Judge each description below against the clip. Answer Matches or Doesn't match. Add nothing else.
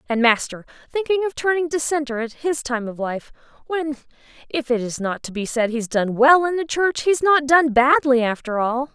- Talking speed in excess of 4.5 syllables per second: Matches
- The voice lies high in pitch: Matches